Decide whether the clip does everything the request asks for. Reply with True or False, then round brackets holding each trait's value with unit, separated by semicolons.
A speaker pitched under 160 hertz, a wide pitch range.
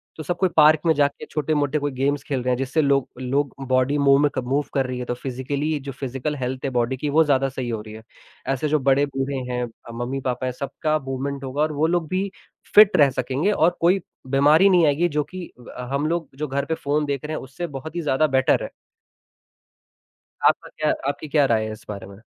False (140 Hz; 2.8 semitones)